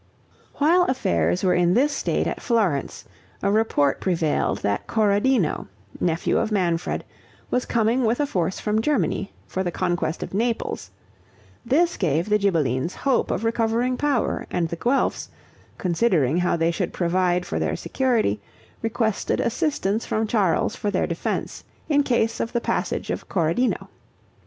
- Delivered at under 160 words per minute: Yes, average, 150 wpm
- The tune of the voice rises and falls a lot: Yes, wide, 5.7 semitones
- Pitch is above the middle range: Yes, high, 205 Hz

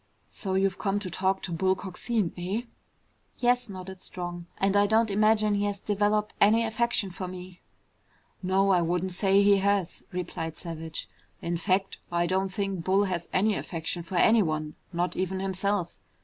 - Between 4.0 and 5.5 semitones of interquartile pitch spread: No, narrow, 2.4 semitones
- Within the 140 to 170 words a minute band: Yes, average, 165 wpm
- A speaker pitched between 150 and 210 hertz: Yes, high, 190 Hz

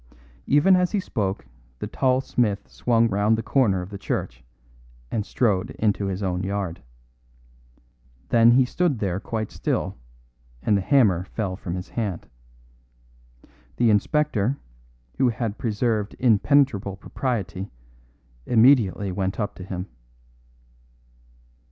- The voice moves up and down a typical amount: Yes, average, 4.0 semitones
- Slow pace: Yes, slow, 125 wpm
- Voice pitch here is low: Yes, low, 105 Hz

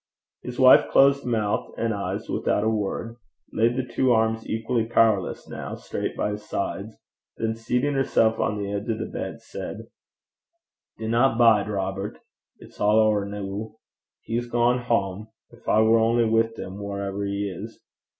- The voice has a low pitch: Yes, low, 110 Hz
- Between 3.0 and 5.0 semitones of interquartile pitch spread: No, narrow, 2.4 semitones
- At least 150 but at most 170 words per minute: Yes, average, 160 wpm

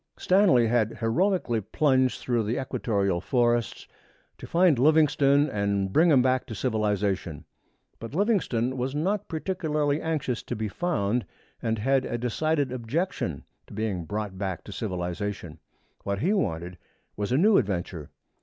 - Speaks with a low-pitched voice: Yes, low, 120 Hz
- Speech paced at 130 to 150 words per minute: Yes, average, 145 wpm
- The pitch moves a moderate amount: No, wide, 6.5 semitones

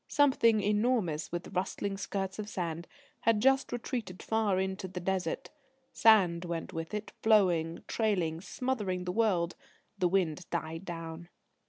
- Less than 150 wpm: Yes, average, 140 wpm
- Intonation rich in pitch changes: No, average, 4.0 semitones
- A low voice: No, high, 190 Hz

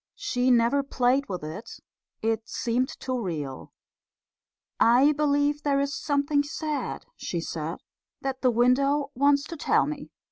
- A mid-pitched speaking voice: No, very high, 270 Hz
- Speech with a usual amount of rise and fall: Yes, average, 3.6 semitones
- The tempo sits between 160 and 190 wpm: No, slow, 135 wpm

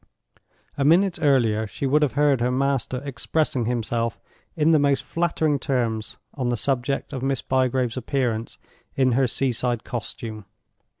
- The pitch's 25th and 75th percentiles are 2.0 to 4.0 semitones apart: Yes, average, 2.9 semitones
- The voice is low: Yes, low, 130 Hz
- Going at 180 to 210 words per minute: No, average, 155 wpm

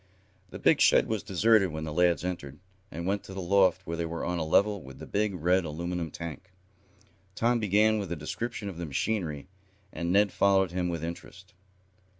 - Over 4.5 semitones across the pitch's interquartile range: No, average, 3.0 semitones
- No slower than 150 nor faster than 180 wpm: No, average, 195 wpm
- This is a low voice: Yes, very low, 90 Hz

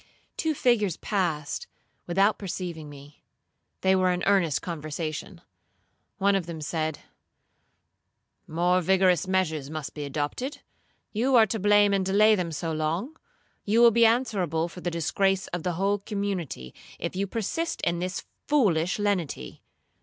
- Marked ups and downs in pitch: No, average, 4.1 semitones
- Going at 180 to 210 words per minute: No, average, 145 wpm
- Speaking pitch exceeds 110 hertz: Yes, medium, 185 Hz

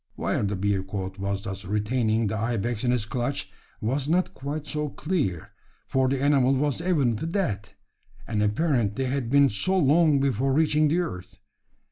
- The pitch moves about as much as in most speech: No, wide, 5.9 semitones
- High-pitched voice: No, low, 130 Hz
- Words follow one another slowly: No, average, 160 wpm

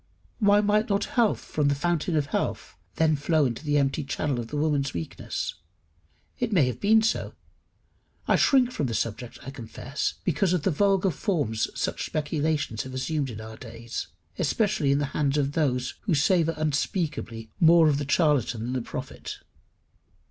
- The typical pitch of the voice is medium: Yes, medium, 150 Hz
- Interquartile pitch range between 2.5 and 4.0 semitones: No, average, 4.9 semitones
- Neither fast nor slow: Yes, average, 175 wpm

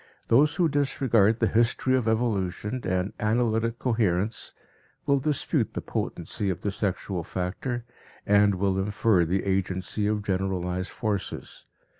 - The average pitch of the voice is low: Yes, low, 105 Hz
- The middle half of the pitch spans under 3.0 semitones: No, average, 3.7 semitones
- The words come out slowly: Yes, slow, 130 wpm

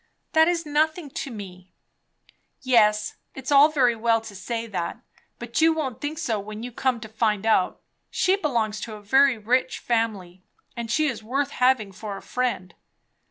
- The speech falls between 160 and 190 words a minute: Yes, average, 175 wpm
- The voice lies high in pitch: Yes, high, 235 Hz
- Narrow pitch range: No, average, 4.6 semitones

